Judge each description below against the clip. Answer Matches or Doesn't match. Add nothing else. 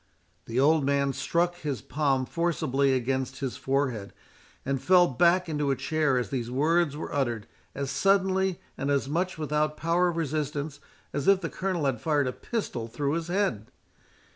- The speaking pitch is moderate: Matches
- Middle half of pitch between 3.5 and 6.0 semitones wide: Matches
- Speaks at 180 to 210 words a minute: Doesn't match